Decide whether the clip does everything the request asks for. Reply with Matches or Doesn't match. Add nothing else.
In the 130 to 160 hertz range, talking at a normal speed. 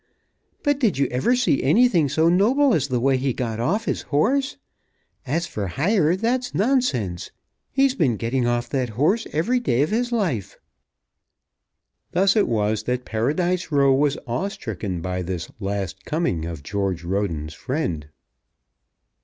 Matches